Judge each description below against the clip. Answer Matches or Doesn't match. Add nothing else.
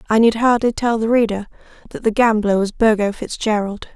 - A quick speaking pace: Doesn't match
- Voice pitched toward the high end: Matches